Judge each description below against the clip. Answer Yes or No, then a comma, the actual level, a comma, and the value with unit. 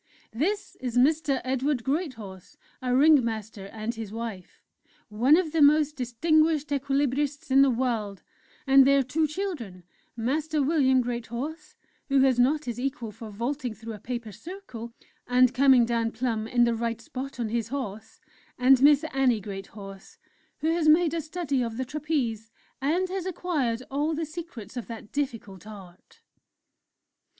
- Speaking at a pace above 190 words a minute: No, average, 155 wpm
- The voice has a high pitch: Yes, very high, 255 Hz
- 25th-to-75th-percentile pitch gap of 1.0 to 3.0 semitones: No, average, 4.6 semitones